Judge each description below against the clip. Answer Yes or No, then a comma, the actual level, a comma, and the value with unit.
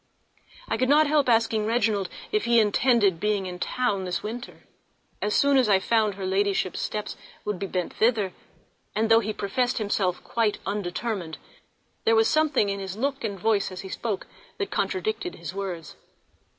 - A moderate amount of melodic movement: Yes, average, 3.4 semitones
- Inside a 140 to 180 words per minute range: Yes, average, 175 wpm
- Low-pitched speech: No, high, 210 Hz